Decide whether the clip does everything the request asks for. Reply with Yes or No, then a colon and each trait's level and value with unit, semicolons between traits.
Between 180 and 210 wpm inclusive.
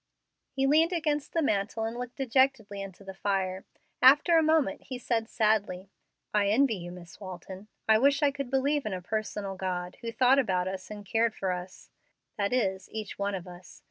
Yes: average, 195 wpm